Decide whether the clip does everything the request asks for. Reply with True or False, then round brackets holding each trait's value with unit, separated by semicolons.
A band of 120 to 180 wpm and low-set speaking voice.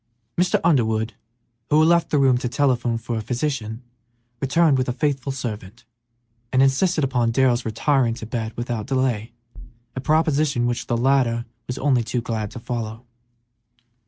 True (160 wpm; 125 Hz)